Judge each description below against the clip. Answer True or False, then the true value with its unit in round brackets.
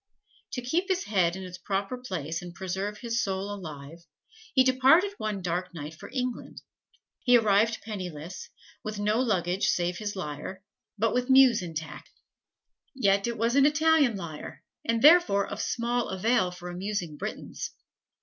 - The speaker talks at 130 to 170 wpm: True (160 wpm)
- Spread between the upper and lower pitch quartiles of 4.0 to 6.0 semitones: True (5.5 semitones)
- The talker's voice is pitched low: False (205 Hz)